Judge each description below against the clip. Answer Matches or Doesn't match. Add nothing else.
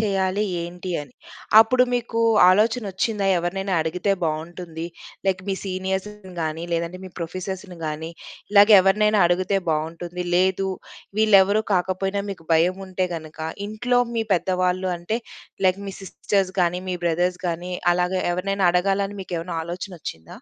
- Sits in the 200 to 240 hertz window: Doesn't match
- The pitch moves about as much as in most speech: Doesn't match